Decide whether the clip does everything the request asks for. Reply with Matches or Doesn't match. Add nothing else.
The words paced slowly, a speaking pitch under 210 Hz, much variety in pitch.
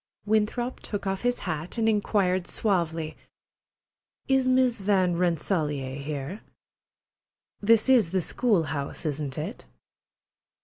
Matches